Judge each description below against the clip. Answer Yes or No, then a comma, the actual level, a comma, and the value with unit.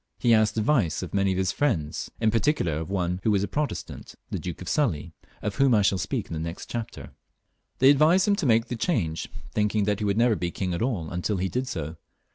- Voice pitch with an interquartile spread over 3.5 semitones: Yes, average, 5.2 semitones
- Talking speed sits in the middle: No, fast, 245 wpm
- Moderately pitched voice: No, low, 105 Hz